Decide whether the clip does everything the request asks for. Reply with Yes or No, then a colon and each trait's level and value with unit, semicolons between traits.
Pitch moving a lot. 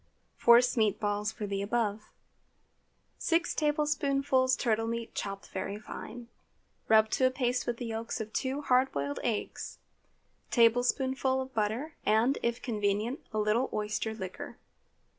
No: average, 3.5 semitones